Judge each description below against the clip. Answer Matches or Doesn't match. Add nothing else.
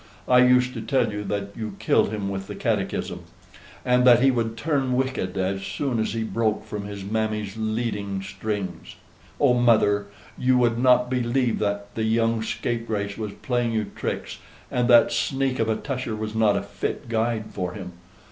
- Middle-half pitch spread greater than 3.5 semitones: Doesn't match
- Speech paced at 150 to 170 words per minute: Doesn't match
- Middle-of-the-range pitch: Doesn't match